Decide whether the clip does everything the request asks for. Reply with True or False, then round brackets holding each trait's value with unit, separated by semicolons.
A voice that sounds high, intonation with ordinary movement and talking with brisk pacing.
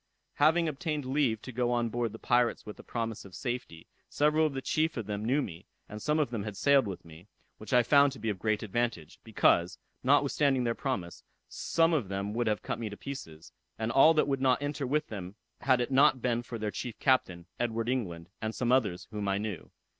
False (120 Hz; 4.7 semitones; 225 wpm)